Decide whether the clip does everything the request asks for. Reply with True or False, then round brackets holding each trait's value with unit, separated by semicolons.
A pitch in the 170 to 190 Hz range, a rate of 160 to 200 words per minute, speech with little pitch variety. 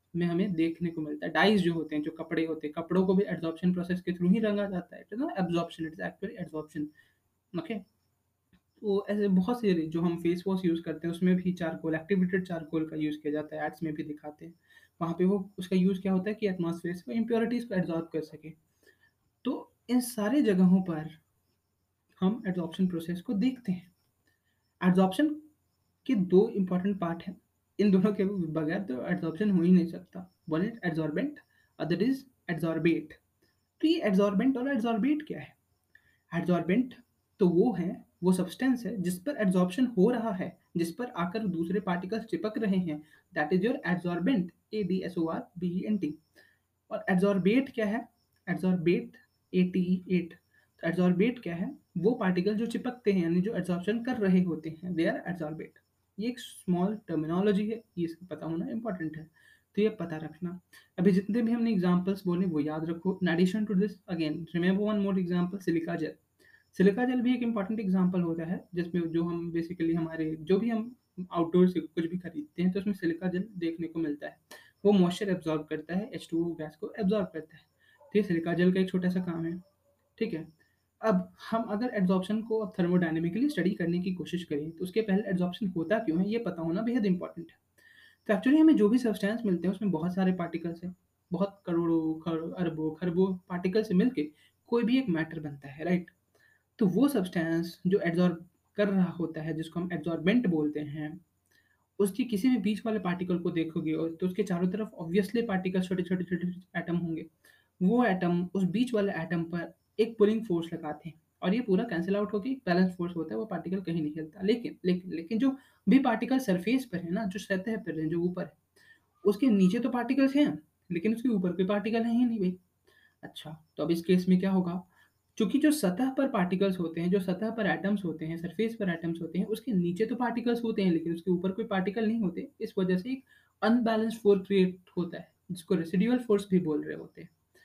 False (185 Hz; 185 wpm; 4.1 semitones)